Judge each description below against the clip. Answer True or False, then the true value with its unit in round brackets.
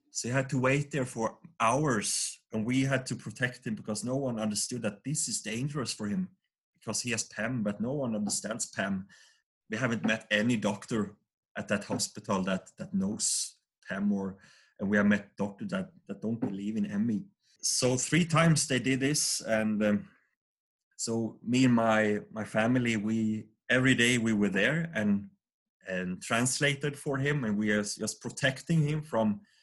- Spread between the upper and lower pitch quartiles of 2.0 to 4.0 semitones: False (5.5 semitones)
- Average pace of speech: True (180 wpm)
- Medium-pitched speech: False (125 Hz)